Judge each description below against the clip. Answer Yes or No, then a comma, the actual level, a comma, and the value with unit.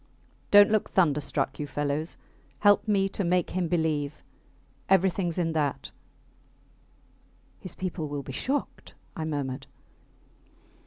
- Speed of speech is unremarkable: No, slow, 115 wpm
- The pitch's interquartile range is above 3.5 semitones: Yes, average, 4.5 semitones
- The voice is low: No, medium, 165 Hz